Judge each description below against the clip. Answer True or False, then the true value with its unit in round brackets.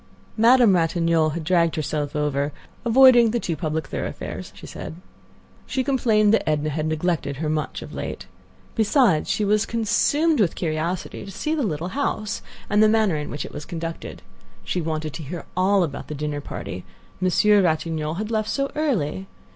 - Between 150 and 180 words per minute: True (175 wpm)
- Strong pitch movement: True (5.8 semitones)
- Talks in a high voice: False (175 Hz)